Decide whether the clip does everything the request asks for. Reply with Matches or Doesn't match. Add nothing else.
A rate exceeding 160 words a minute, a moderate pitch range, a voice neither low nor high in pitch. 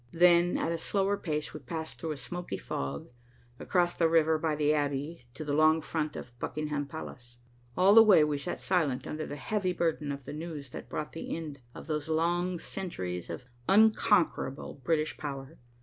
Matches